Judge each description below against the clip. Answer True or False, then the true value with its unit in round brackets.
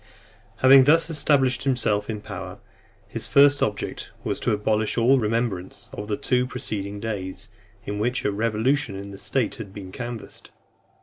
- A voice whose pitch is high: False (110 Hz)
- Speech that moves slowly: False (165 wpm)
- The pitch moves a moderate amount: True (3.9 semitones)